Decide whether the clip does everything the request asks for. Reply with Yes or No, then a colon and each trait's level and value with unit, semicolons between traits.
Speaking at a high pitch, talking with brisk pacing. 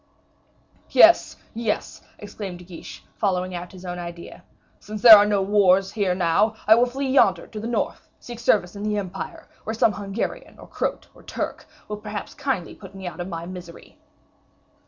No: high, 200 Hz; average, 180 wpm